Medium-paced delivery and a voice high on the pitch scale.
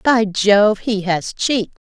Yes: average, 155 wpm; high, 210 Hz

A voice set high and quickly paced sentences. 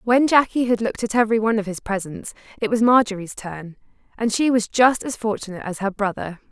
Yes: high, 215 Hz; fast, 210 wpm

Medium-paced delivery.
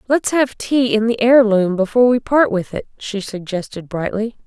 Yes: average, 190 wpm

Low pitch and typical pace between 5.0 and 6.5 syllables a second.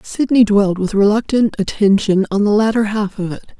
No: high, 210 Hz; 5.1 syllables/s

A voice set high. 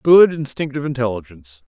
No: low, 130 Hz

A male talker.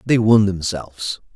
Yes: male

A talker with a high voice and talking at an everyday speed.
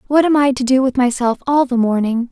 No: very high, 255 Hz; fast, 260 wpm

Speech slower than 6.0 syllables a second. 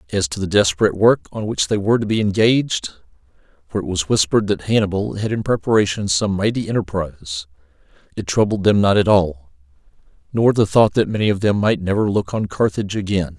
No: 6.1 syllables/s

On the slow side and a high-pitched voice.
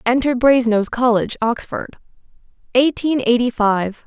Yes: slow, 105 wpm; high, 240 Hz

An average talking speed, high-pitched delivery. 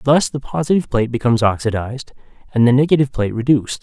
No: average, 170 wpm; low, 125 Hz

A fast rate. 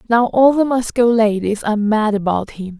No: average, 195 wpm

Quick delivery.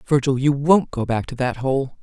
Yes: fast, 235 wpm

